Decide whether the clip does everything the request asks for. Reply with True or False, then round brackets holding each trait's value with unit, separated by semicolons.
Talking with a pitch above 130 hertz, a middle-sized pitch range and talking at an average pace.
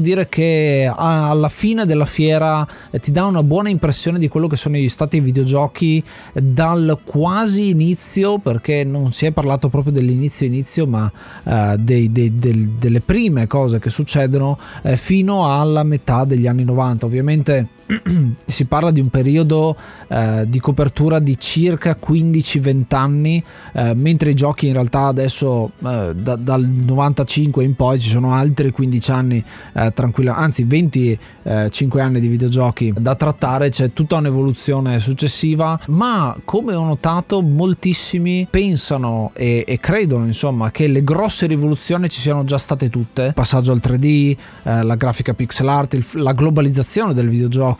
True (140 Hz; 3.8 semitones; 155 wpm)